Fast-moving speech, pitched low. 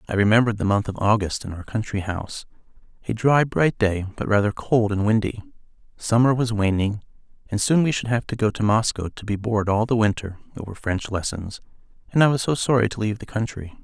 Yes: fast, 215 wpm; low, 110 Hz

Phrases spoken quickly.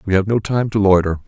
Yes: fast, 280 wpm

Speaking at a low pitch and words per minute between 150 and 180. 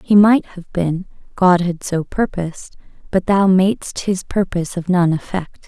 No: medium, 180 Hz; average, 170 wpm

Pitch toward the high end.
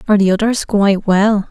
Yes: high, 205 Hz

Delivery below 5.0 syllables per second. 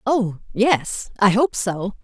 Yes: 3.1 syllables/s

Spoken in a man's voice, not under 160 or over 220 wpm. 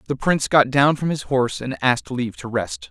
No: male; fast, 250 wpm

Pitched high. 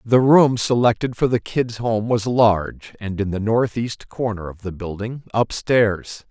No: low, 110 Hz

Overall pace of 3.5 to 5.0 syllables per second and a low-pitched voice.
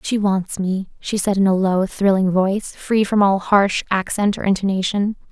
No: 4.7 syllables/s; high, 195 Hz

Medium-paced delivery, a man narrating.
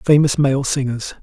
Yes: average, 145 wpm; male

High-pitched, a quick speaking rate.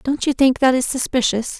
Yes: very high, 260 Hz; fast, 225 wpm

